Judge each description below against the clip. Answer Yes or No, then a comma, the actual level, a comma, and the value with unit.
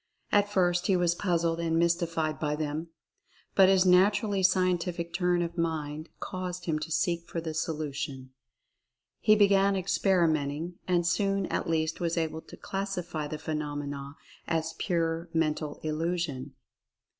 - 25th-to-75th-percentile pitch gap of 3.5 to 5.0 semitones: No, narrow, 2.5 semitones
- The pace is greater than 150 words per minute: No, average, 145 wpm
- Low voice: No, medium, 170 Hz